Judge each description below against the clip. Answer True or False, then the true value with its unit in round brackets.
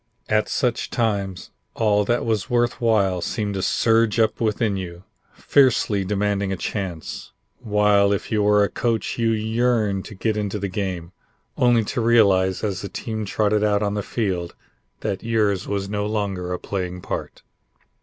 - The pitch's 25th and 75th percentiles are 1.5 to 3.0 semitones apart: True (2.4 semitones)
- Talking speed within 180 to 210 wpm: False (165 wpm)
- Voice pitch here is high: False (105 Hz)